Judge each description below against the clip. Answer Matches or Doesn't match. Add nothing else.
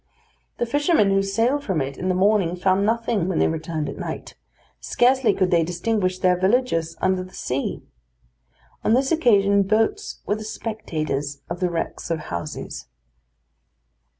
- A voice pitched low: Doesn't match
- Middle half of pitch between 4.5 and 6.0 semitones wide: Matches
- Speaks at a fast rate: Doesn't match